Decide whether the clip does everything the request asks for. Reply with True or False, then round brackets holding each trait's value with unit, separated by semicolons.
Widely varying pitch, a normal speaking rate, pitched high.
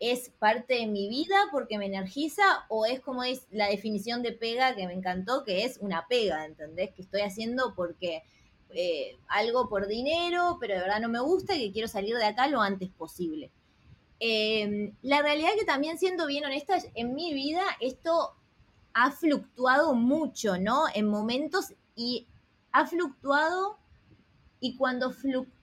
True (6.1 semitones; 170 wpm; 245 Hz)